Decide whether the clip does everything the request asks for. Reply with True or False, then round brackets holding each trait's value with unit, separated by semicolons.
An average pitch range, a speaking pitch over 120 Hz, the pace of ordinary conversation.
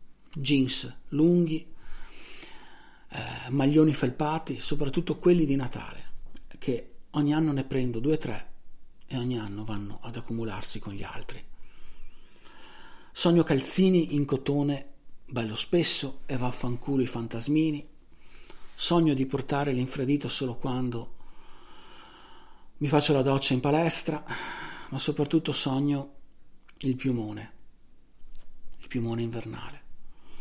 False (3.8 semitones; 140 Hz; 110 wpm)